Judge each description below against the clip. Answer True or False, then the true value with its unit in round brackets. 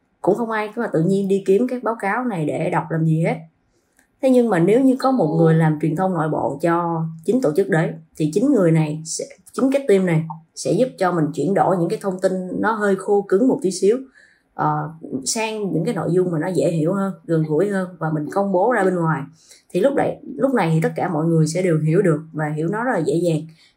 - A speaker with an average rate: False (265 wpm)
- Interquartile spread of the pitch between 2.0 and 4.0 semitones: True (3.7 semitones)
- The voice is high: False (175 Hz)